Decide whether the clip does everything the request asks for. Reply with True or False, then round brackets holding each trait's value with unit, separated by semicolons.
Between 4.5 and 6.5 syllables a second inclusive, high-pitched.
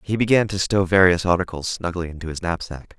False (5.9 syllables/s; 90 Hz)